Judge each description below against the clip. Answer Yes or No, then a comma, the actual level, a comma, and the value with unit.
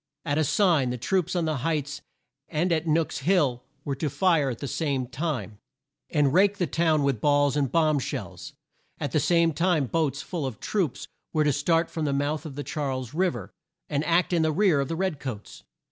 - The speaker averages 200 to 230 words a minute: Yes, fast, 205 wpm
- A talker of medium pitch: Yes, medium, 150 Hz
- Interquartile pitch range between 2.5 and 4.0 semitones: Yes, average, 3.2 semitones